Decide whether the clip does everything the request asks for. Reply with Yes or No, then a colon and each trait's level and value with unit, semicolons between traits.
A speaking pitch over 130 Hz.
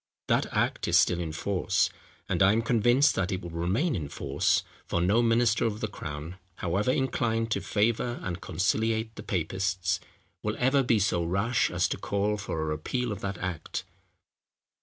No: low, 100 Hz